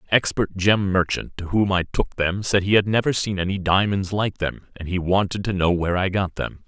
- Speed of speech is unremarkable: No, fast, 245 wpm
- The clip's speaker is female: No, male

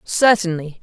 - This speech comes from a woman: Yes, female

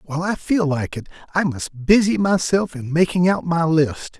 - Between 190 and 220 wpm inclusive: Yes, average, 200 wpm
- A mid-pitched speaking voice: Yes, medium, 165 Hz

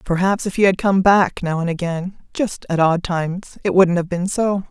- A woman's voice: Yes, female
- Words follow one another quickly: Yes, fast, 230 wpm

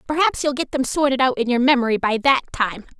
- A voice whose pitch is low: No, very high, 265 Hz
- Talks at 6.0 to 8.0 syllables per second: Yes, 6.1 syllables/s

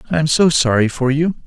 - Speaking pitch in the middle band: Yes, medium, 145 Hz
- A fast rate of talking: Yes, fast, 245 wpm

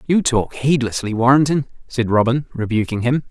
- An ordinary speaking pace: Yes, average, 145 wpm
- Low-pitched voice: Yes, low, 125 Hz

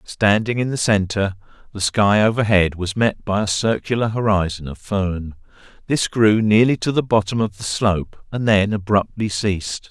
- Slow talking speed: No, average, 170 wpm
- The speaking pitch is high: No, low, 105 Hz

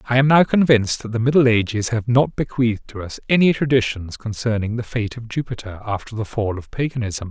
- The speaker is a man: Yes, male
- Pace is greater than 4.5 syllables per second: Yes, 5.9 syllables/s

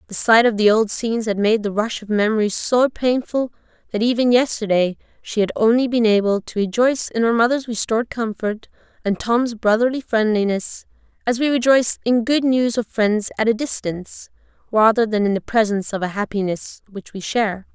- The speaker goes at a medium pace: Yes, average, 185 wpm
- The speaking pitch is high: Yes, high, 225 Hz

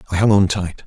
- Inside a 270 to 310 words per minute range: Yes, fast, 280 wpm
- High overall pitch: No, very low, 95 Hz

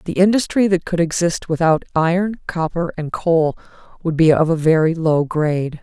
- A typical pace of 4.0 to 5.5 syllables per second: Yes, 5.0 syllables/s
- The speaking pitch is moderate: Yes, medium, 165 Hz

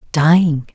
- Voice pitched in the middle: Yes, medium, 160 Hz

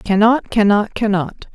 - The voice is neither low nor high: No, high, 210 Hz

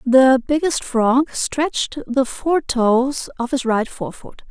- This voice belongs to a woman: Yes, female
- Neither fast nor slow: Yes, average, 145 wpm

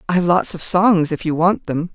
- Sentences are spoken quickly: Yes, fast, 280 wpm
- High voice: No, medium, 175 Hz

